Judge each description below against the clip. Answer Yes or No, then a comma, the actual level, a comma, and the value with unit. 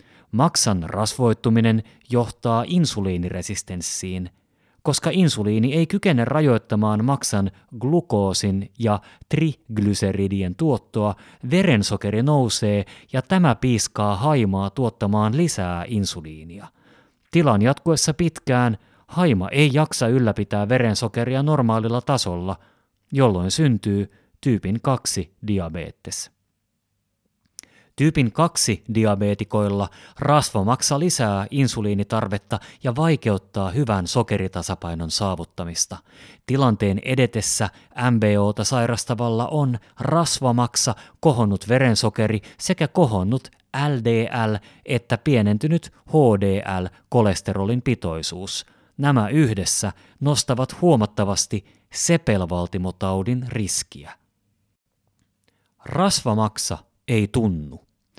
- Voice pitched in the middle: No, low, 110 Hz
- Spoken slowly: Yes, slow, 75 wpm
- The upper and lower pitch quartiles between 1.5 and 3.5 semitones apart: No, average, 4.8 semitones